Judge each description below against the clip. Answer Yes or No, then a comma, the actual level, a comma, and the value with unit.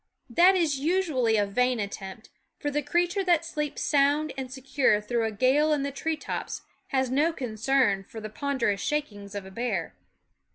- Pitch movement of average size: No, wide, 5.7 semitones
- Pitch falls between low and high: No, very high, 265 Hz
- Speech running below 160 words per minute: No, average, 180 wpm